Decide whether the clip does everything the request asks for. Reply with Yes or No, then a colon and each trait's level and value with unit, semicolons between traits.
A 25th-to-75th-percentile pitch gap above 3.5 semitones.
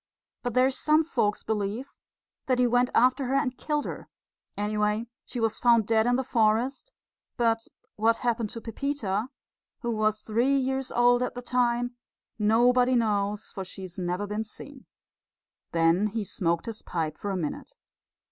No: average, 3.1 semitones